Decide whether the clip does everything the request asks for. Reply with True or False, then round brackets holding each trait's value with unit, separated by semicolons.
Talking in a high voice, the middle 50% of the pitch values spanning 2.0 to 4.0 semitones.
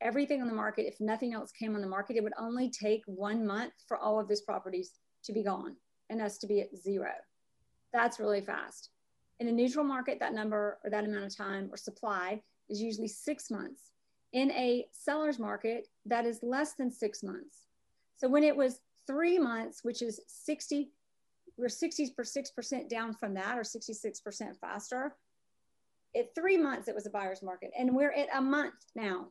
False (230 Hz; 4.4 semitones)